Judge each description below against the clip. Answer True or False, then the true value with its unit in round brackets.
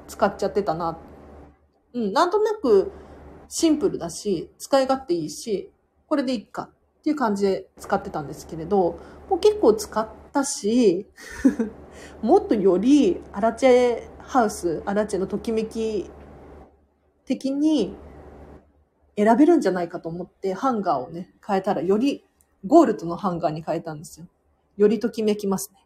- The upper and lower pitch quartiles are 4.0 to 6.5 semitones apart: False (8.1 semitones)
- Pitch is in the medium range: False (210 Hz)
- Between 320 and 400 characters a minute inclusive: False (310 characters per minute)